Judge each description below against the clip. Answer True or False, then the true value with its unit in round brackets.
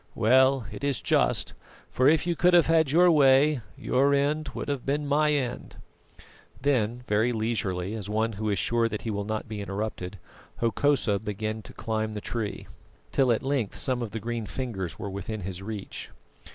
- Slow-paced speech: False (185 wpm)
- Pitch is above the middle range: False (115 Hz)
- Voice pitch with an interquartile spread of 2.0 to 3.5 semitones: False (4.8 semitones)